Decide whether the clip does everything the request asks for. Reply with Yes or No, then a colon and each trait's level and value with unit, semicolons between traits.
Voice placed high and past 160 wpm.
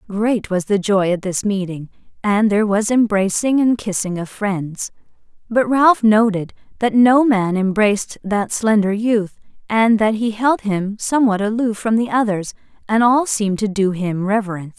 Yes: high, 210 Hz; average, 170 wpm